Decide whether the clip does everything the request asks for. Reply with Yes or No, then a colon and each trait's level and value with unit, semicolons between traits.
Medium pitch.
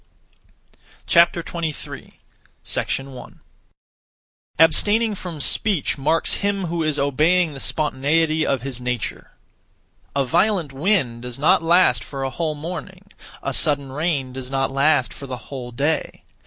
Yes: medium, 150 Hz